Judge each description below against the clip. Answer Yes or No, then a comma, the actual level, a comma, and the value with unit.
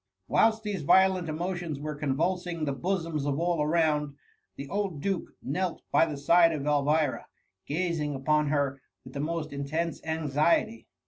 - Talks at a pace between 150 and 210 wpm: Yes, average, 160 wpm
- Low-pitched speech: No, medium, 155 Hz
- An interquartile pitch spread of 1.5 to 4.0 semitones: Yes, average, 3.2 semitones